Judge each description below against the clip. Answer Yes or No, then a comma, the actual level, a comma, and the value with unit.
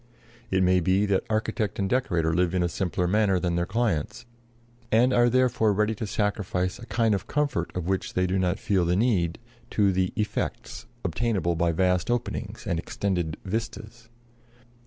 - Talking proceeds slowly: No, average, 175 wpm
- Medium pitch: No, very low, 95 Hz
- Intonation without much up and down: No, average, 3.6 semitones